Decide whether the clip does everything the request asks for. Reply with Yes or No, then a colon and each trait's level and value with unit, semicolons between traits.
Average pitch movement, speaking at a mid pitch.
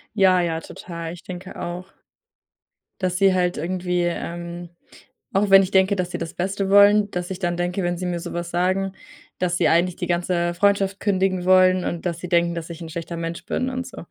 No: narrow, 1.6 semitones; medium, 180 Hz